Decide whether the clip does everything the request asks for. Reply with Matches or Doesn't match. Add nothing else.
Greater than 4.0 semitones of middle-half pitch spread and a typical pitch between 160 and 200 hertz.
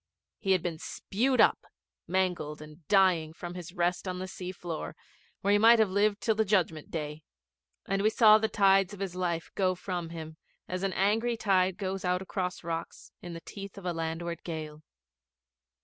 Doesn't match